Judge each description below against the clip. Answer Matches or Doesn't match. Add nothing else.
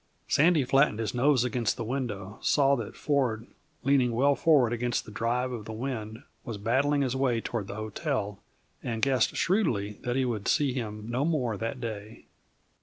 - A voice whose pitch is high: Doesn't match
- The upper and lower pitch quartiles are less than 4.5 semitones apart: Matches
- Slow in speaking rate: Doesn't match